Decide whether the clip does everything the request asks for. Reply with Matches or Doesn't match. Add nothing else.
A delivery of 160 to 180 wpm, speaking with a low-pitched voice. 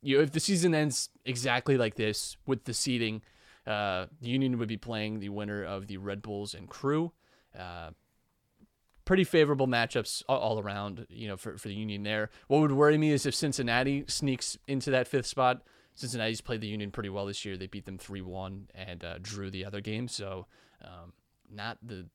Doesn't match